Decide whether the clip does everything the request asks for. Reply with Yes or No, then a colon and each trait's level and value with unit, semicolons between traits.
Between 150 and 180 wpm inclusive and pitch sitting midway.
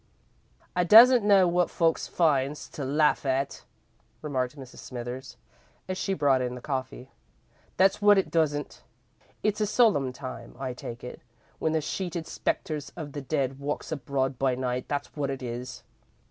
Yes: average, 160 wpm; medium, 145 Hz